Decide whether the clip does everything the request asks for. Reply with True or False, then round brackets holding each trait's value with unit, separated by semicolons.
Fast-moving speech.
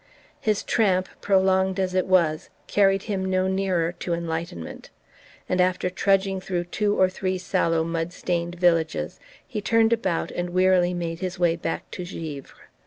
False (160 wpm)